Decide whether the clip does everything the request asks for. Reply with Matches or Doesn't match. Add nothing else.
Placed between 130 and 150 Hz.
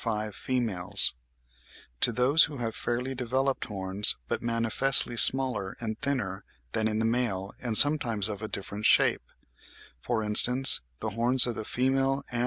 Doesn't match